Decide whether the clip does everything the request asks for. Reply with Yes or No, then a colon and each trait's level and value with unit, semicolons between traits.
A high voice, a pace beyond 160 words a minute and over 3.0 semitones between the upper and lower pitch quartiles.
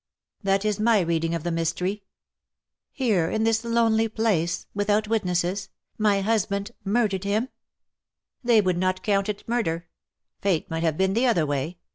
Yes: high, 200 Hz; average, 190 wpm; average, 4.0 semitones